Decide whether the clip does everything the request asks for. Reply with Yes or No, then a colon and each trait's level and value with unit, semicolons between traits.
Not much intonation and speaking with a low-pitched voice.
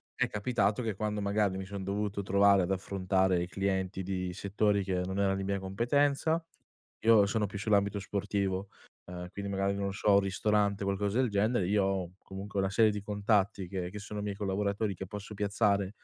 Yes: narrow, 1.3 semitones; low, 100 Hz